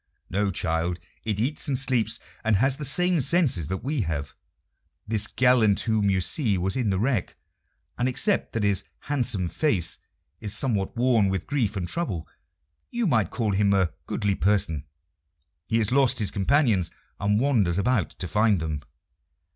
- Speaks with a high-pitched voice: No, low, 105 Hz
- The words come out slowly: No, average, 165 wpm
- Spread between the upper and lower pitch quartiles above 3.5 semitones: Yes, average, 5.1 semitones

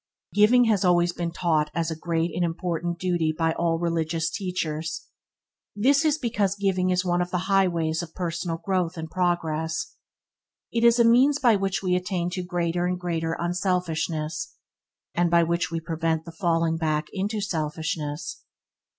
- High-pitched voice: No, medium, 175 Hz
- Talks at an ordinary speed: Yes, average, 170 wpm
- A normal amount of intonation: No, narrow, 2.2 semitones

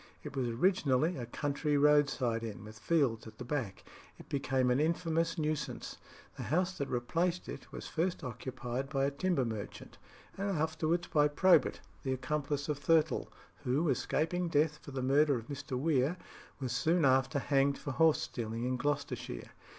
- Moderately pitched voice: Yes, medium, 145 Hz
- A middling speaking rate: Yes, average, 165 wpm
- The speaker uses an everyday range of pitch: Yes, average, 3.8 semitones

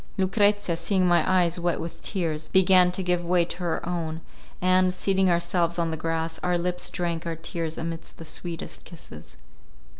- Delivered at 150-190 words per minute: Yes, average, 175 wpm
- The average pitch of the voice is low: No, medium, 175 Hz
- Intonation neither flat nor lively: No, narrow, 1.7 semitones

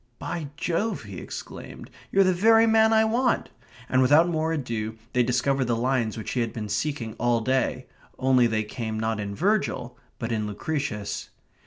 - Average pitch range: No, wide, 6.6 semitones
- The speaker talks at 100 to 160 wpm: No, average, 175 wpm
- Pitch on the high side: No, low, 125 Hz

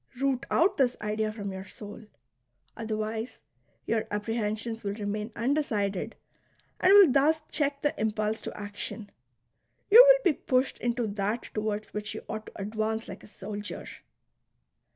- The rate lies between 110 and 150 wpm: Yes, average, 145 wpm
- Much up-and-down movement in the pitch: No, average, 3.7 semitones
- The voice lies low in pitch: No, high, 220 Hz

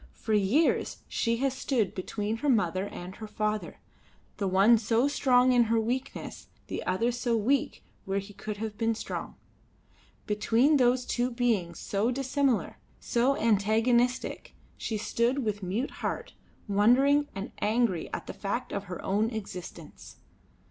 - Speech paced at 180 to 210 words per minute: No, average, 150 wpm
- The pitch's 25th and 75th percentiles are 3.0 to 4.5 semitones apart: Yes, average, 3.3 semitones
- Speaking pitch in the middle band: No, high, 225 Hz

